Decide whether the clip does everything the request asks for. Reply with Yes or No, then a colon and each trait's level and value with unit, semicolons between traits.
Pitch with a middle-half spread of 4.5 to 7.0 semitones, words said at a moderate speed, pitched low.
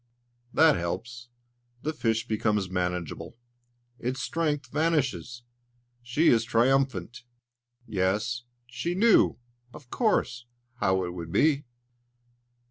No: average, 5.2 semitones; slow, 100 wpm; low, 120 Hz